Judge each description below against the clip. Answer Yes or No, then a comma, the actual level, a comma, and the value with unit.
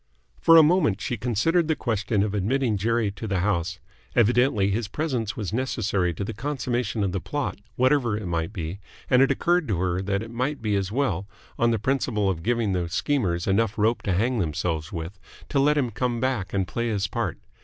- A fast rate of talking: Yes, fast, 210 wpm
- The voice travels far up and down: No, average, 4.6 semitones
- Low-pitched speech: Yes, low, 110 Hz